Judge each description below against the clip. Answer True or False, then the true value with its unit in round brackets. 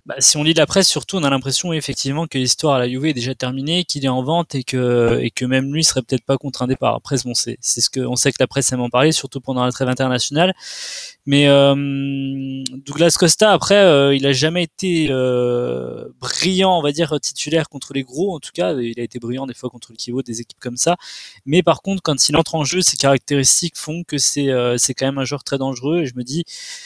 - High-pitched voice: False (140 Hz)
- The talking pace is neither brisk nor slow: False (255 wpm)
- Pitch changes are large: False (3.8 semitones)